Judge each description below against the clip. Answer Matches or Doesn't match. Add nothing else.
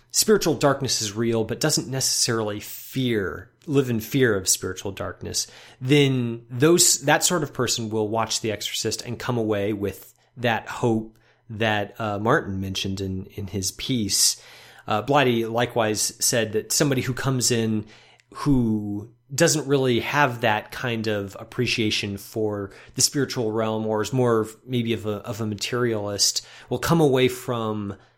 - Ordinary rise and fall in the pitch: Matches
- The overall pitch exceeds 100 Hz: Matches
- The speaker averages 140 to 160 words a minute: Matches